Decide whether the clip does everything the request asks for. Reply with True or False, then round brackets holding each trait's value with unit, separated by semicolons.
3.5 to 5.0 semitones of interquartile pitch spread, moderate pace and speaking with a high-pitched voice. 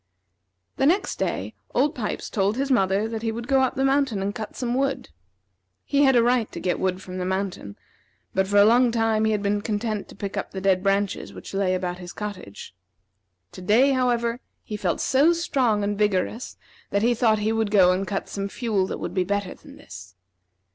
False (3.8 semitones; 215 wpm; 210 Hz)